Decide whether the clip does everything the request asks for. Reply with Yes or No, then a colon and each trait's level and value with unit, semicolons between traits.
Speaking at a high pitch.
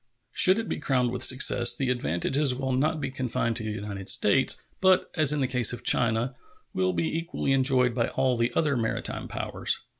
No: low, 125 Hz